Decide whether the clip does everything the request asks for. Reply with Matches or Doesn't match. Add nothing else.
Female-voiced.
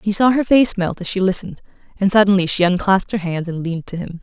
Matches